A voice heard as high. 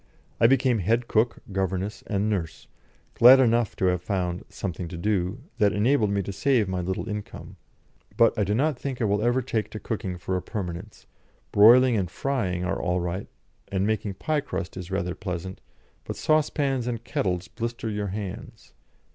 No: low, 105 Hz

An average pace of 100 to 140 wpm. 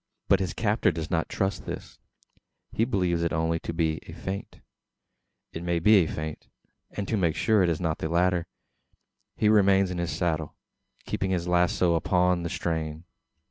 No: average, 180 wpm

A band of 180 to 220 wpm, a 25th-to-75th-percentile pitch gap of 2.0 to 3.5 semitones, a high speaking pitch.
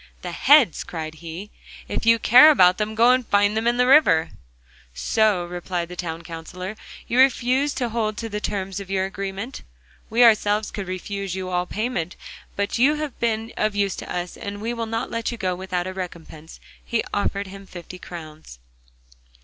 No: average, 190 wpm; average, 4.2 semitones; high, 200 Hz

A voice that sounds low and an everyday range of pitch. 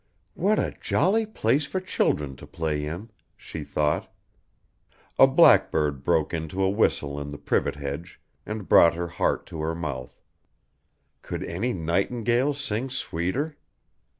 No: very low, 85 Hz; wide, 7.9 semitones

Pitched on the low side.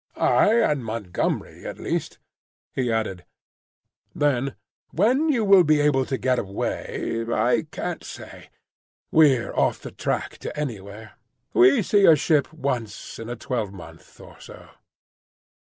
Yes: low, 130 Hz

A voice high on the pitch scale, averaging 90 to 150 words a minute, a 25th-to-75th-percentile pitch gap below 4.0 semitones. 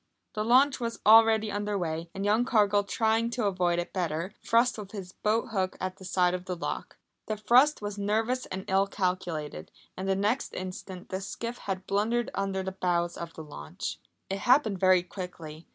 No: high, 195 Hz; average, 190 wpm; average, 3.3 semitones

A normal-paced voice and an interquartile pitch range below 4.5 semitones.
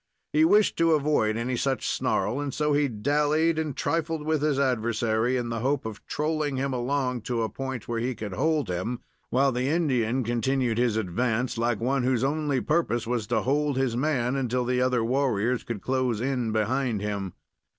Yes: average, 190 wpm; average, 3.5 semitones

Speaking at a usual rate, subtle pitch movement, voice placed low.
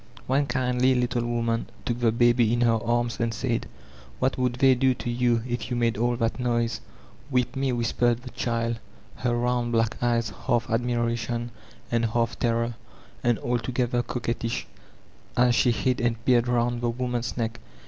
Yes: average, 170 wpm; narrow, 1.0 semitones; low, 120 Hz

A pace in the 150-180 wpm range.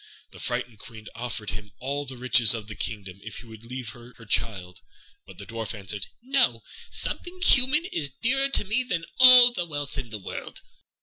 No: average, 195 wpm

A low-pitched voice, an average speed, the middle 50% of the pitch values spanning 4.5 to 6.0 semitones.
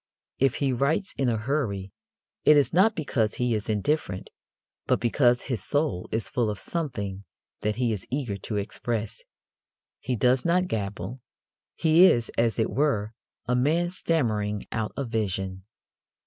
Yes: low, 120 Hz; average, 155 wpm; average, 5.3 semitones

